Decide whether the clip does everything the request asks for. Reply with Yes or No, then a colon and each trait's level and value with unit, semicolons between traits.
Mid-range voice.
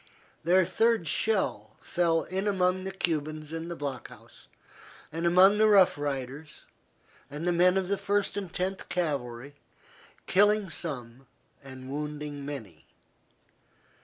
Yes: medium, 165 Hz